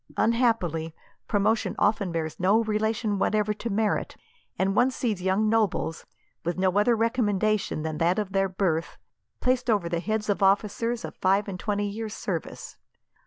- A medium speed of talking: Yes, average, 160 wpm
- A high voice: Yes, high, 205 Hz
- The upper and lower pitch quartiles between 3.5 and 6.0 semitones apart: No, average, 2.9 semitones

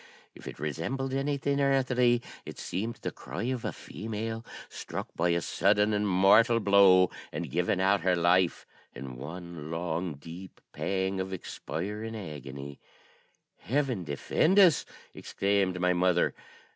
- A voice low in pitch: Yes, very low, 95 Hz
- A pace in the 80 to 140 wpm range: Yes, slow, 135 wpm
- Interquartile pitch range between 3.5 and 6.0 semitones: Yes, average, 4.7 semitones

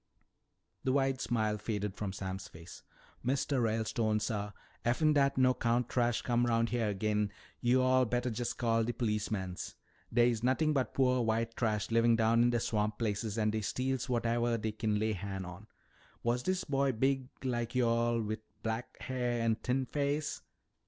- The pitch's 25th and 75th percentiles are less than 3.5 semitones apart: Yes, average, 2.8 semitones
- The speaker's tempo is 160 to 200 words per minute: Yes, average, 170 wpm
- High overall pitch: No, low, 115 Hz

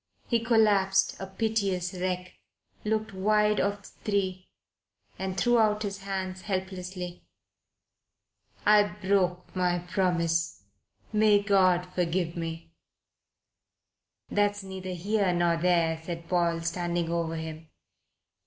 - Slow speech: Yes, slow, 110 wpm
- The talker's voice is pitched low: No, medium, 185 Hz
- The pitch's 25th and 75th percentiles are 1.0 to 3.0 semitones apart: Yes, average, 2.7 semitones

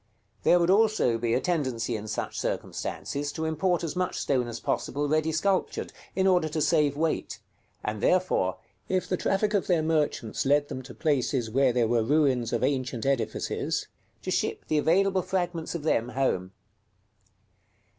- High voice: No, medium, 145 Hz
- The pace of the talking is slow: No, average, 165 wpm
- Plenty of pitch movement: Yes, wide, 5.9 semitones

